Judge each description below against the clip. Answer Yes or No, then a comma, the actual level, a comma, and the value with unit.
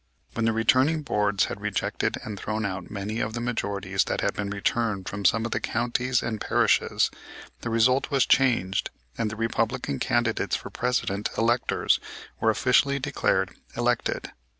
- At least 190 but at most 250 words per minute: No, average, 160 wpm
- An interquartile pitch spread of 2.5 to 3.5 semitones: Yes, average, 3.2 semitones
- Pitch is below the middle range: Yes, low, 115 Hz